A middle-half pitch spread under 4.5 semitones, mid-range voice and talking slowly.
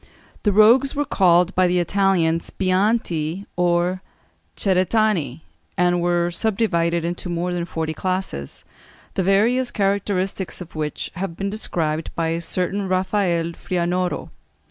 Yes: narrow, 2.6 semitones; medium, 180 Hz; slow, 125 wpm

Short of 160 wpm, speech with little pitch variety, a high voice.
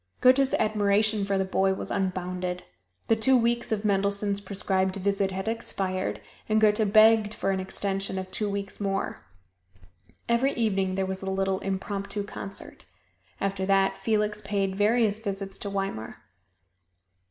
Yes: average, 145 wpm; narrow, 1.9 semitones; high, 200 Hz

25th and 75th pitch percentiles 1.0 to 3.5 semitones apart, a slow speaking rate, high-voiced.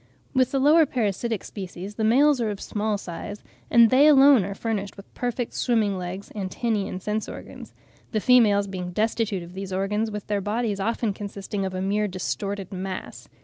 No: average, 3.1 semitones; average, 185 wpm; high, 210 Hz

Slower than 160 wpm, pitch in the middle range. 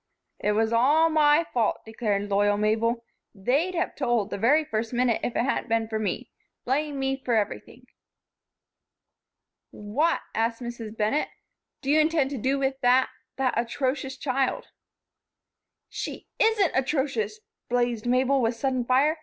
No: average, 145 wpm; very high, 250 Hz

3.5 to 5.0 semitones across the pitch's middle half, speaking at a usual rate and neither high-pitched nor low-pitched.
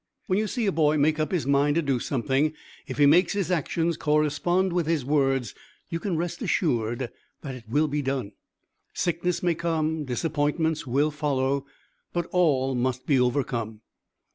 Yes: average, 3.8 semitones; average, 170 wpm; medium, 150 Hz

